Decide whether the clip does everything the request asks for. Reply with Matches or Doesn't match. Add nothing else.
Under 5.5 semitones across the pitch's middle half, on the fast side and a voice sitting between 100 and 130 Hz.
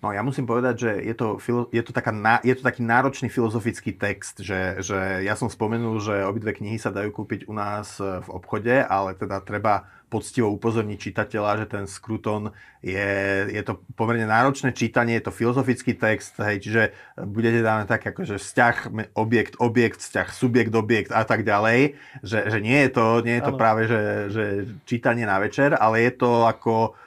Matches